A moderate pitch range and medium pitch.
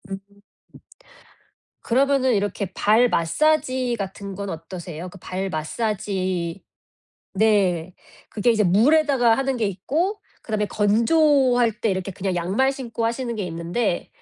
No: average, 4.9 semitones; high, 210 Hz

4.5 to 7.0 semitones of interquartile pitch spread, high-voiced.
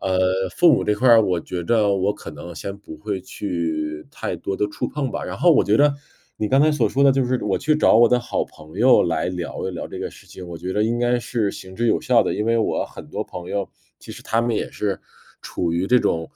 No: average, 5.0 semitones; low, 105 Hz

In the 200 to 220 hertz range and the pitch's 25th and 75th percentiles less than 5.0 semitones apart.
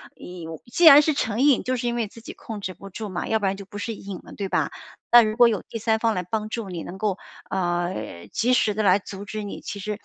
Yes: high, 210 Hz; average, 3.1 semitones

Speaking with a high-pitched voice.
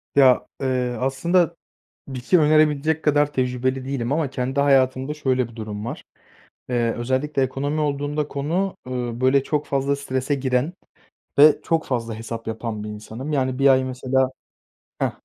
No: low, 130 Hz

